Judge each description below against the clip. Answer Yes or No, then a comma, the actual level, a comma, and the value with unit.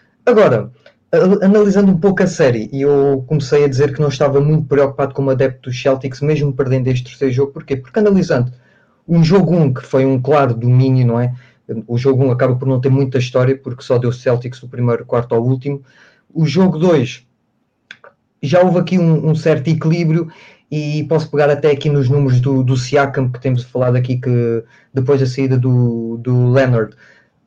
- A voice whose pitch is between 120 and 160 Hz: Yes, low, 135 Hz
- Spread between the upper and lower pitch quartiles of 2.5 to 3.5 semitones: Yes, average, 3.1 semitones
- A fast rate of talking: Yes, fast, 190 wpm